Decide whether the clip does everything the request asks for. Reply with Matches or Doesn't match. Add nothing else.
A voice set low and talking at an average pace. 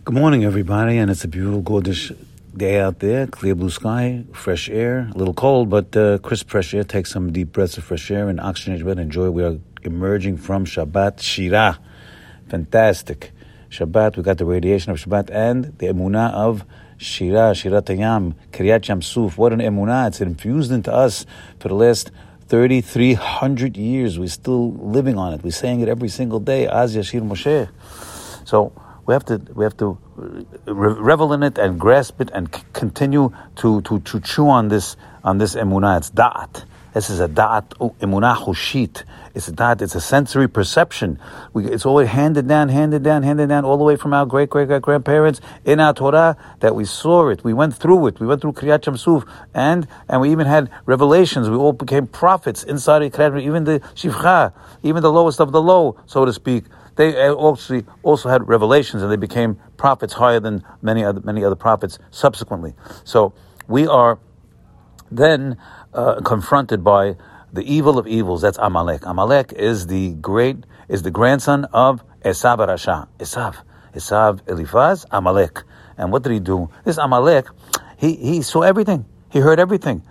Matches